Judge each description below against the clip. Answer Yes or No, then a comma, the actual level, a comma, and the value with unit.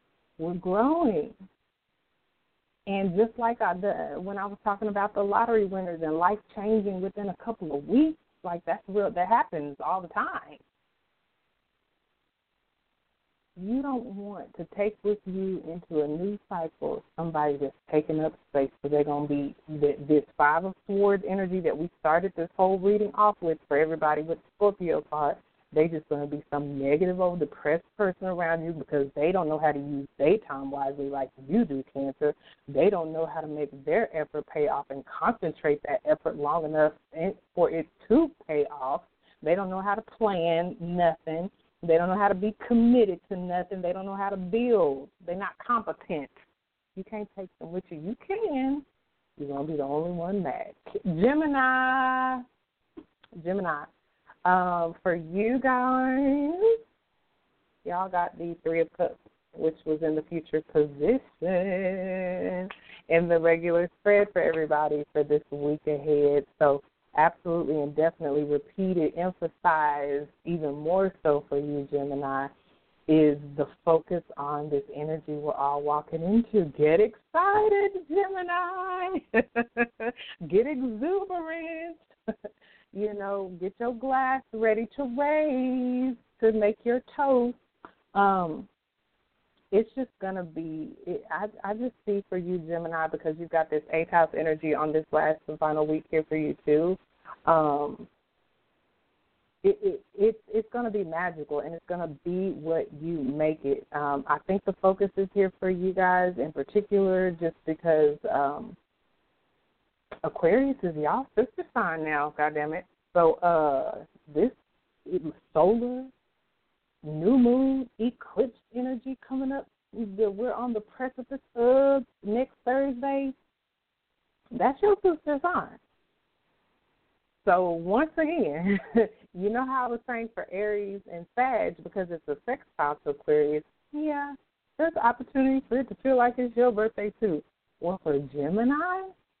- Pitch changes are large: Yes, wide, 7.0 semitones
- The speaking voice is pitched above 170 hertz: Yes, medium, 185 Hz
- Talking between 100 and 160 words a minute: Yes, average, 150 wpm